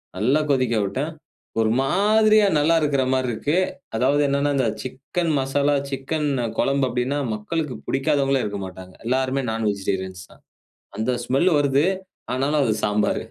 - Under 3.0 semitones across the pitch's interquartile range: No, average, 4.1 semitones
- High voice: No, low, 135 Hz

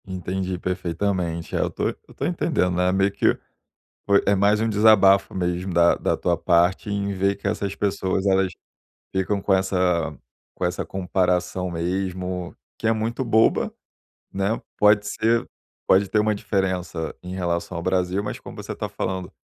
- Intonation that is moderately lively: No, narrow, 1.9 semitones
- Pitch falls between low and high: No, very low, 95 Hz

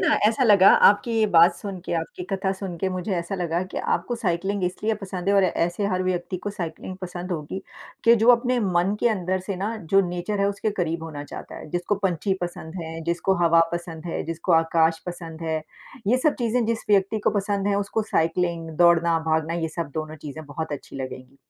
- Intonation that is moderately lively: Yes, average, 3.2 semitones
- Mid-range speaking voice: Yes, medium, 180 Hz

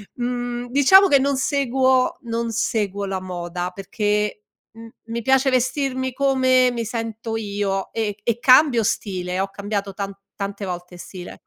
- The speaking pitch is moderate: No, high, 225 Hz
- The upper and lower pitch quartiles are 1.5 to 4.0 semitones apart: No, average, 4.5 semitones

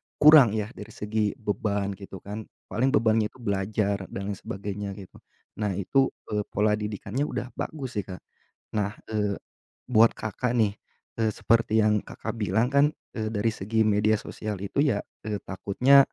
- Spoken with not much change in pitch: Yes, narrow, 2.1 semitones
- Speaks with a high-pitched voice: No, low, 105 Hz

